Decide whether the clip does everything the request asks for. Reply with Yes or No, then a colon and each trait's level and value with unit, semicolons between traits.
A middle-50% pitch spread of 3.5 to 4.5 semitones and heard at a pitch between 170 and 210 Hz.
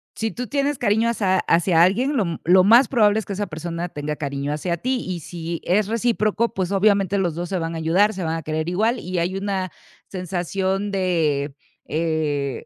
Yes: average, 4.1 semitones; medium, 185 Hz